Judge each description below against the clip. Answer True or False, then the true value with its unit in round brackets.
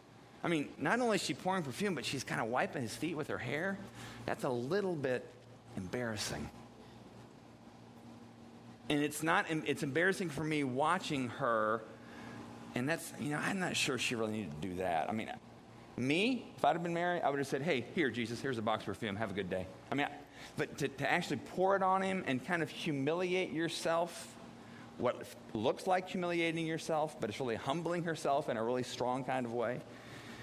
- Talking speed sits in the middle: True (195 wpm)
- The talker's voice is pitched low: False (145 Hz)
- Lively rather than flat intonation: True (6.1 semitones)